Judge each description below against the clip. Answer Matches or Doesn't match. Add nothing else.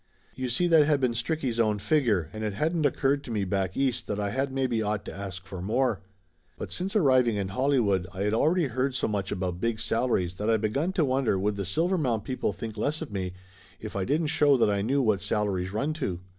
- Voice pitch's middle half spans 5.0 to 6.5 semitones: Matches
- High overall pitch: Doesn't match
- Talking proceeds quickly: Matches